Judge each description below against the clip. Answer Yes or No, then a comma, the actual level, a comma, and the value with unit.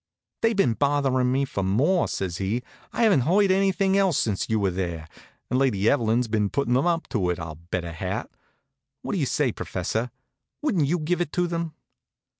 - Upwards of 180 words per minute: Yes, average, 200 wpm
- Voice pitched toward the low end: Yes, low, 130 Hz